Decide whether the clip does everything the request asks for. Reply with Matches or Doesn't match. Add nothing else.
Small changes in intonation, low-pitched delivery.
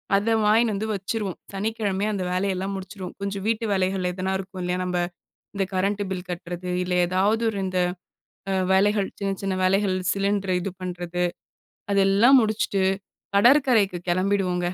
Doesn't match